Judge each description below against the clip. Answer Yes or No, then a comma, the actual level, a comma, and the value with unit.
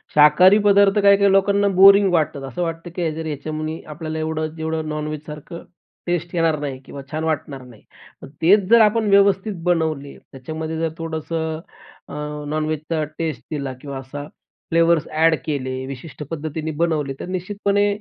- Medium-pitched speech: Yes, medium, 160 Hz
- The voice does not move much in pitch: No, average, 3.0 semitones